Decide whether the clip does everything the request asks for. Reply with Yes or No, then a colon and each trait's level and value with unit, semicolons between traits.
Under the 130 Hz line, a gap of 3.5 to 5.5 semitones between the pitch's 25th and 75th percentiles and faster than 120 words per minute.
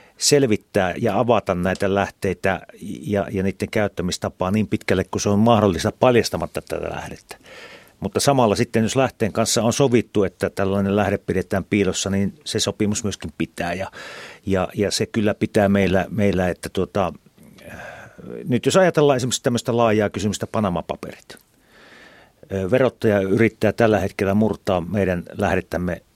No: low, 105 Hz; average, 2.7 semitones; average, 140 wpm